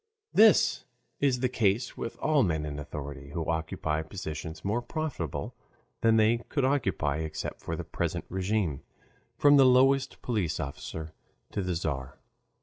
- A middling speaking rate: Yes, average, 145 wpm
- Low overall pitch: Yes, very low, 95 Hz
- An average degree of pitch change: No, wide, 8.2 semitones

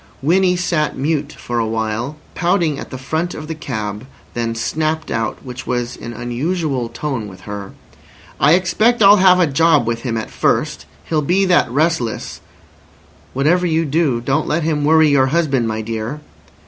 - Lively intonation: Yes, wide, 5.7 semitones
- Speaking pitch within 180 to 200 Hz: No, medium, 145 Hz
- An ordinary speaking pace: Yes, average, 175 wpm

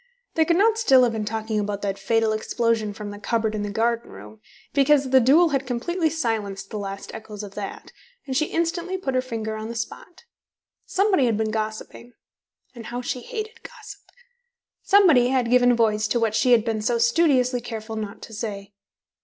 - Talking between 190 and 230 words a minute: Yes, average, 195 wpm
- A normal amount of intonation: Yes, average, 3.7 semitones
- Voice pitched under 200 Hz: No, high, 230 Hz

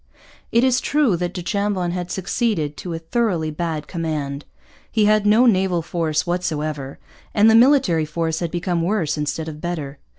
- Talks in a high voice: No, medium, 175 Hz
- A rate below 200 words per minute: Yes, average, 170 wpm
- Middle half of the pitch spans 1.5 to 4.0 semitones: No, average, 4.7 semitones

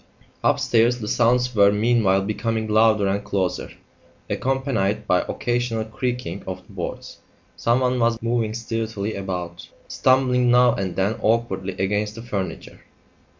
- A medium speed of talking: No, slow, 130 wpm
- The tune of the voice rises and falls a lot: No, average, 3.3 semitones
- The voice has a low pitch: Yes, low, 110 Hz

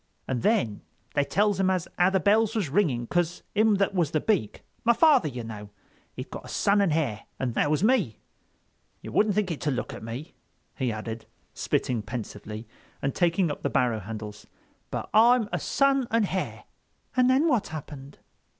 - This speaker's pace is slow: No, average, 185 wpm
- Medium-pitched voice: Yes, medium, 165 Hz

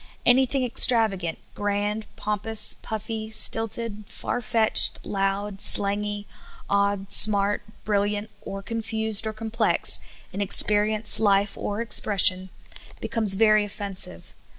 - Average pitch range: No, narrow, 1.7 semitones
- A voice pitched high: Yes, high, 210 Hz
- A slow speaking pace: Yes, slow, 110 wpm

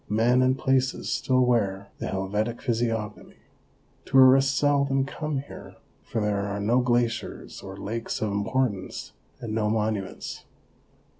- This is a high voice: No, low, 115 Hz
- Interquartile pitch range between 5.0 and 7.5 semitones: No, average, 3.8 semitones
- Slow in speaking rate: Yes, slow, 130 wpm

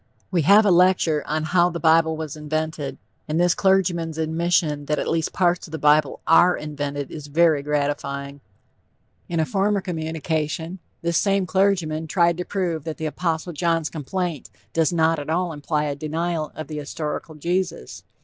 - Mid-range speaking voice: Yes, medium, 160 Hz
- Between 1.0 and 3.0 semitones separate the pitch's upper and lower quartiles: Yes, narrow, 2.5 semitones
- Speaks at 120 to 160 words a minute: No, average, 170 wpm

